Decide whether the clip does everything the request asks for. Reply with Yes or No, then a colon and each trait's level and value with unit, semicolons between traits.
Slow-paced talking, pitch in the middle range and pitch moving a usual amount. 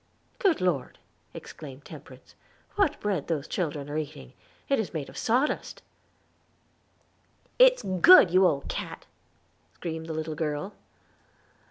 No: slow, 125 wpm; medium, 165 Hz; wide, 6.0 semitones